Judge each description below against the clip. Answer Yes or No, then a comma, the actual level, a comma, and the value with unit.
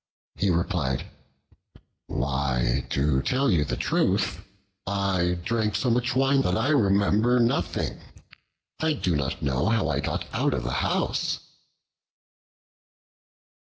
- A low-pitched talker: Yes, very low, 95 Hz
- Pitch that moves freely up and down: Yes, wide, 8.4 semitones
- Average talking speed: No, slow, 120 wpm